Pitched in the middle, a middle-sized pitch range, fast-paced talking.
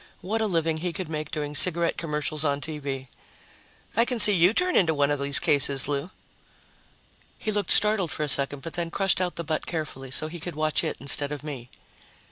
Yes: medium, 155 Hz; average, 3.7 semitones; fast, 210 wpm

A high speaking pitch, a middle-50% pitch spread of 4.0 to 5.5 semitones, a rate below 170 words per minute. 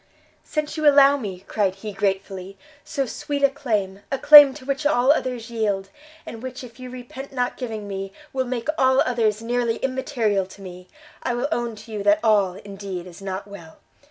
No: high, 230 Hz; average, 4.8 semitones; average, 190 wpm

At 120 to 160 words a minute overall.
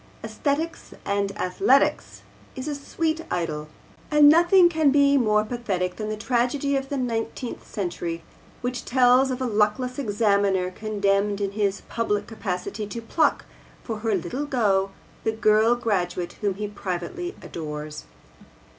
Yes: average, 140 wpm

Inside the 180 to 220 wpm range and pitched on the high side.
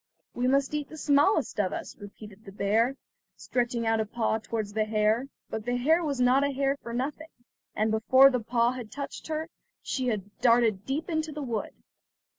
Yes: average, 195 wpm; high, 245 Hz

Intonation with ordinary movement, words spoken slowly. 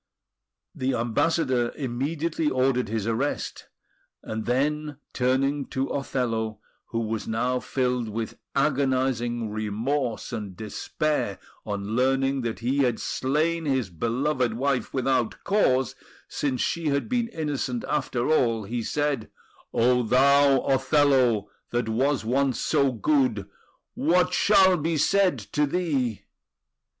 Yes: average, 3.7 semitones; slow, 120 wpm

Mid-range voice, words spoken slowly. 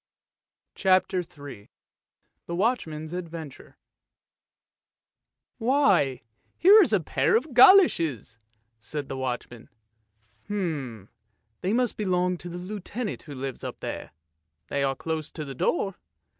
Yes: medium, 170 Hz; slow, 115 wpm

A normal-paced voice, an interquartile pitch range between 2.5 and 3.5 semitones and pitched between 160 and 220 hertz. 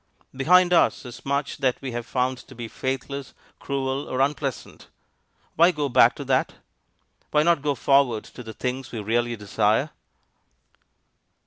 No: average, 150 wpm; average, 2.8 semitones; low, 135 Hz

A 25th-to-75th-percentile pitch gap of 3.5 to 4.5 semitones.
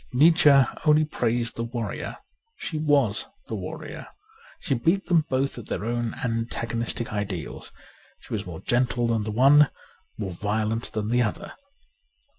Yes: average, 4.0 semitones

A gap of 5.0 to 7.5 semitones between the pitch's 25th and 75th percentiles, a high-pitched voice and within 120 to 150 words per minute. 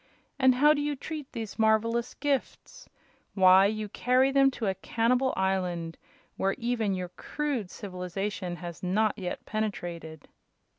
Yes: wide, 5.4 semitones; high, 215 Hz; average, 140 wpm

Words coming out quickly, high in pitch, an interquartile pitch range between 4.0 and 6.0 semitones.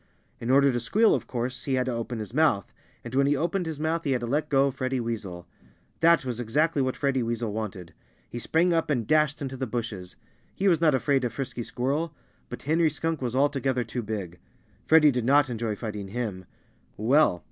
No: fast, 210 wpm; low, 130 Hz; average, 4.3 semitones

